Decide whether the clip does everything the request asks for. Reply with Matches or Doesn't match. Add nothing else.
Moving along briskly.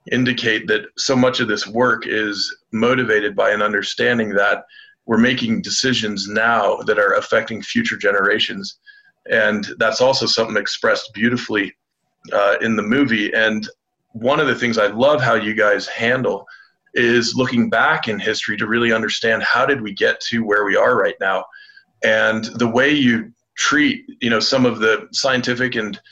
Doesn't match